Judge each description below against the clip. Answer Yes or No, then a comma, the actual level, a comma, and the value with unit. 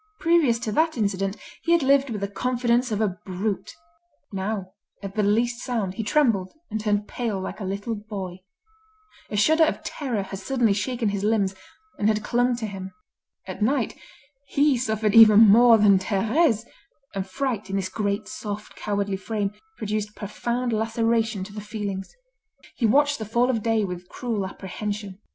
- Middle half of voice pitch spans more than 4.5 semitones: No, average, 3.0 semitones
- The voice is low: No, high, 215 Hz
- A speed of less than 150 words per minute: No, average, 170 wpm